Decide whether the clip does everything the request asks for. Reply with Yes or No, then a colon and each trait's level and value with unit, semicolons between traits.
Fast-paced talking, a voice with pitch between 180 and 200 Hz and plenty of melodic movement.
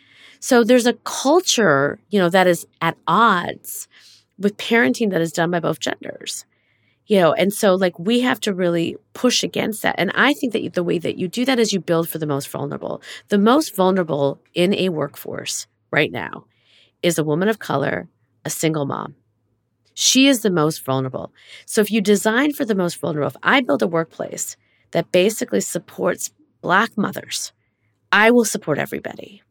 No: average, 185 wpm; medium, 185 Hz; wide, 6.2 semitones